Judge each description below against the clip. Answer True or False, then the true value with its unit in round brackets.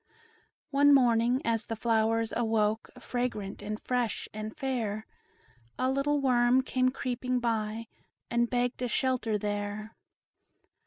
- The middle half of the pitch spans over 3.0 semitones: False (2.7 semitones)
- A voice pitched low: False (235 Hz)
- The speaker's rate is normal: False (120 wpm)